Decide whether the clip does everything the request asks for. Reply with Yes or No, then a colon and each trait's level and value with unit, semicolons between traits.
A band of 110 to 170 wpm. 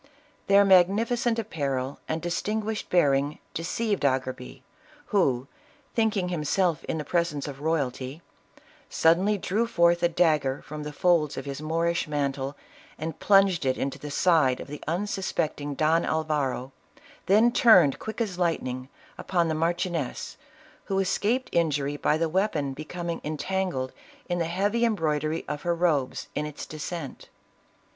Yes: average, 140 wpm